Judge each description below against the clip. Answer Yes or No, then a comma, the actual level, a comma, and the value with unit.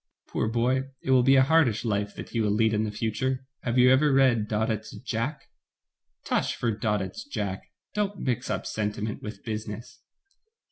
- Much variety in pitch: No, average, 3.6 semitones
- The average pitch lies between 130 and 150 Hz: No, low, 115 Hz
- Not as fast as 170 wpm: No, average, 180 wpm